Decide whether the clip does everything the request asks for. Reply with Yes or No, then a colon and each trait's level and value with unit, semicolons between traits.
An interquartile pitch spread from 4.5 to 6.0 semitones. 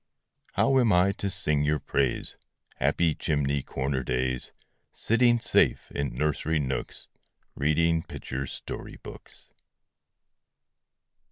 No: average, 4.0 semitones